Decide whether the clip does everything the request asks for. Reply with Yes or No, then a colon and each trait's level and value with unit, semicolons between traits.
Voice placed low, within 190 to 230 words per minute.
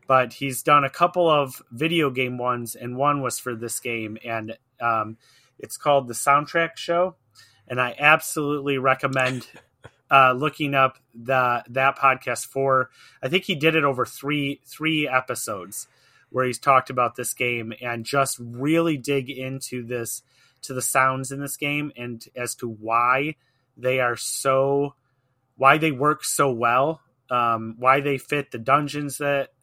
No: low, 130 Hz; average, 160 wpm